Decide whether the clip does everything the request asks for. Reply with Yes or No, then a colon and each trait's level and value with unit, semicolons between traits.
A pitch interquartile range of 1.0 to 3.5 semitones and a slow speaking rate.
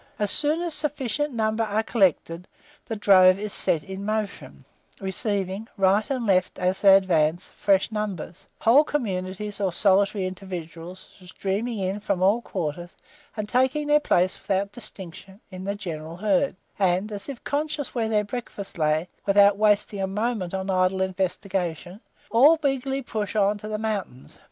No: average, 2.8 semitones; average, 160 wpm